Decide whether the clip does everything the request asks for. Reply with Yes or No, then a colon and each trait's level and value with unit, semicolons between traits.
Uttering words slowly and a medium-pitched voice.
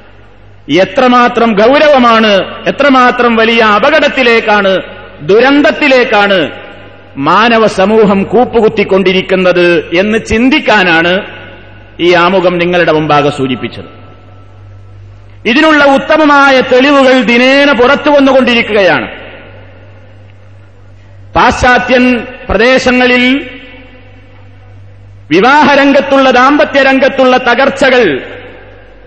No: slow, 55 wpm; high, 215 Hz